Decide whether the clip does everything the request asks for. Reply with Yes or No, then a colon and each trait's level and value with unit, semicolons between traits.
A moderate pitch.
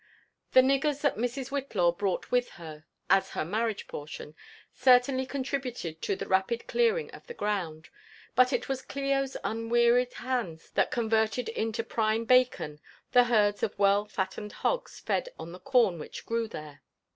No: high, 230 Hz